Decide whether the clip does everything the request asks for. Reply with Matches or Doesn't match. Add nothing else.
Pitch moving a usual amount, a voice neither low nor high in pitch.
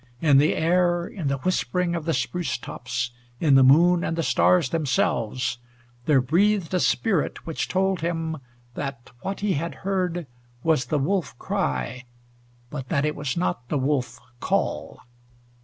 Matches